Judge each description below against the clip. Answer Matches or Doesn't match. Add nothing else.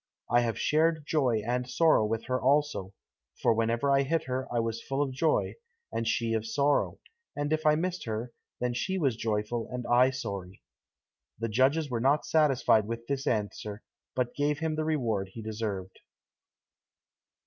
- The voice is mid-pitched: Doesn't match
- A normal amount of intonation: Matches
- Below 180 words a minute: Matches